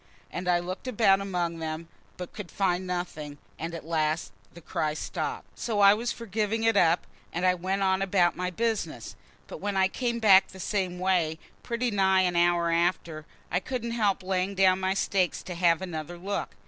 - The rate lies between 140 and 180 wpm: No, average, 195 wpm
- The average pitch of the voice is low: No, medium, 185 Hz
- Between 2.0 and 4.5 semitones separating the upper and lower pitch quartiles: Yes, narrow, 2.5 semitones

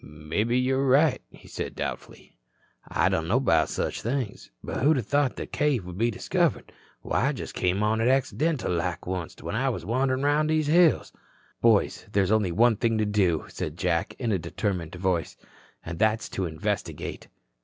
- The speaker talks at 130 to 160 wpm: No, average, 180 wpm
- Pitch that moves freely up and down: Yes, wide, 6.5 semitones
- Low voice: Yes, low, 110 Hz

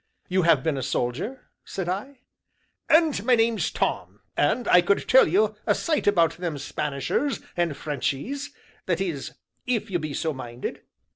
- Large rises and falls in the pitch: Yes, wide, 7.6 semitones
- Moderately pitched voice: Yes, medium, 180 Hz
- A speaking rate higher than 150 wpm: Yes, average, 160 wpm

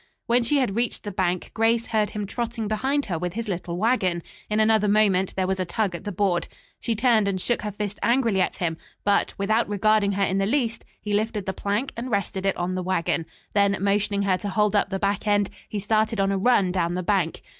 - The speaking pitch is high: Yes, high, 205 Hz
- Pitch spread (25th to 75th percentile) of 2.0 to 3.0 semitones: Yes, narrow, 2.4 semitones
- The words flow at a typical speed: No, fast, 235 wpm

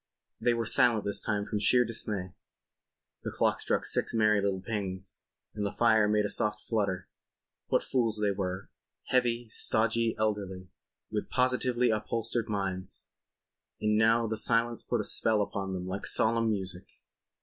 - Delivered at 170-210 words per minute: No, average, 150 wpm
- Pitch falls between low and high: No, low, 105 Hz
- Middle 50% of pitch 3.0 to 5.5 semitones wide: No, narrow, 2.6 semitones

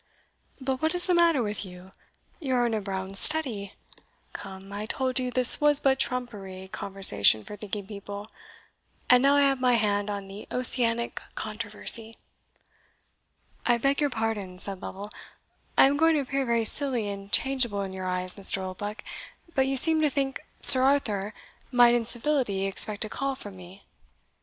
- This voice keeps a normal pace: Yes, average, 170 wpm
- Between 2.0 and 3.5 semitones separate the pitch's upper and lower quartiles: No, average, 5.1 semitones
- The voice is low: No, high, 225 Hz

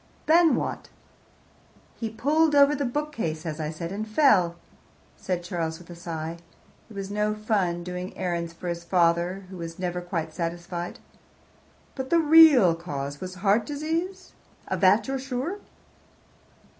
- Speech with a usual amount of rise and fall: No, wide, 7.5 semitones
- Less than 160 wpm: Yes, average, 150 wpm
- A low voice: No, medium, 185 Hz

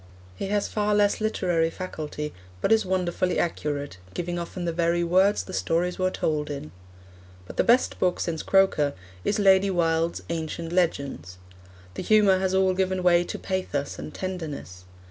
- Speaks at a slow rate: No, average, 165 wpm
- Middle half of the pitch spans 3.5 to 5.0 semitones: No, average, 2.8 semitones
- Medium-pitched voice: Yes, medium, 175 Hz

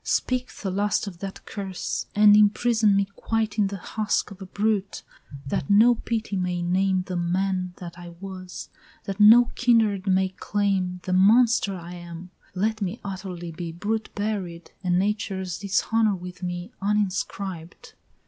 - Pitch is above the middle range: Yes, high, 195 Hz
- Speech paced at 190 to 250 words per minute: No, average, 155 wpm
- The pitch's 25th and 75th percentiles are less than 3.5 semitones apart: Yes, narrow, 2.6 semitones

